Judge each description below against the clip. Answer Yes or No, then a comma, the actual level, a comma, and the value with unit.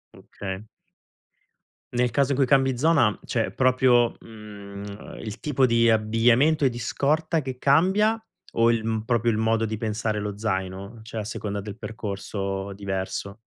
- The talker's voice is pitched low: Yes, low, 115 Hz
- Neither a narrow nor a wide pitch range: Yes, average, 3.8 semitones